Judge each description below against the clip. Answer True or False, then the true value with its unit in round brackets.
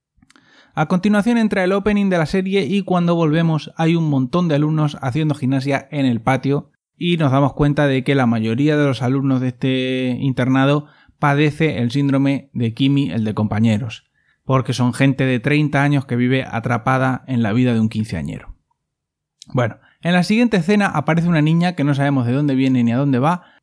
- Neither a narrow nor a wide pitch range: True (3.5 semitones)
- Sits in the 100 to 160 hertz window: True (140 Hz)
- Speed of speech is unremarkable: False (195 wpm)